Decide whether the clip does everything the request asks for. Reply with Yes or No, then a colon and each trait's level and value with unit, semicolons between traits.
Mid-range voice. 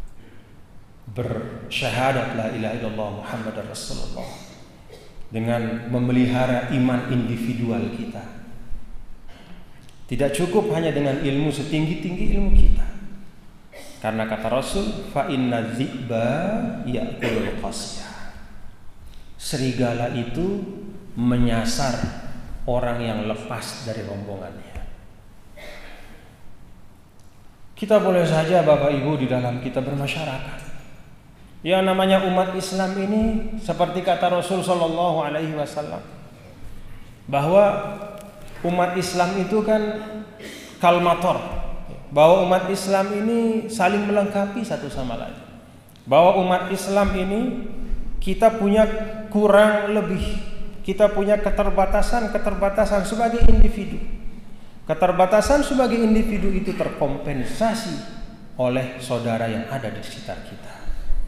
Yes: medium, 155 Hz